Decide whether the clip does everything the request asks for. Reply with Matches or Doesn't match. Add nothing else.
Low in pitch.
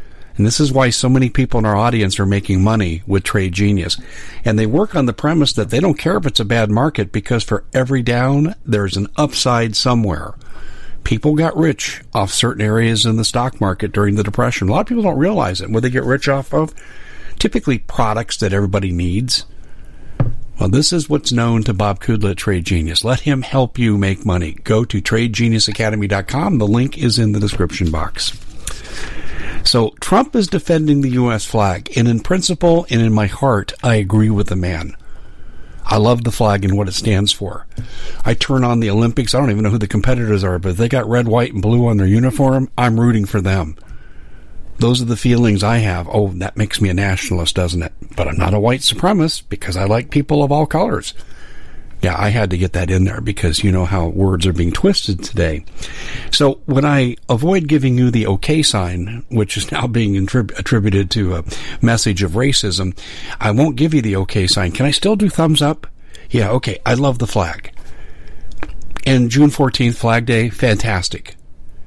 Matches